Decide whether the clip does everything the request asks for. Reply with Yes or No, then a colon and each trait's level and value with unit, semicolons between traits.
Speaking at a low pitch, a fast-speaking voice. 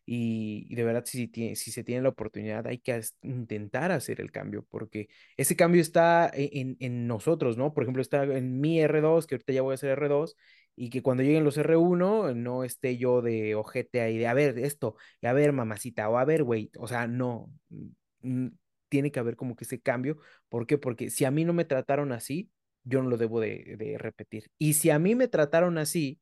Yes: low, 130 Hz; fast, 225 wpm